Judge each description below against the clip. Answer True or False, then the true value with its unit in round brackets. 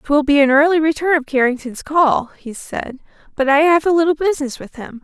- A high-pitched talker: True (290 Hz)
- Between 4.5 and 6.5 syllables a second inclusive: True (5.5 syllables/s)